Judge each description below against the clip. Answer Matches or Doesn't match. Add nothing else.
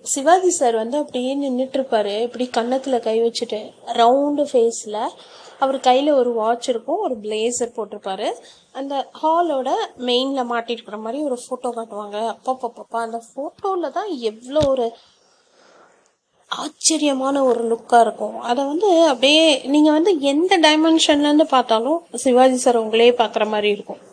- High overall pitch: Matches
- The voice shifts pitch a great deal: Doesn't match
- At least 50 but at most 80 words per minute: Doesn't match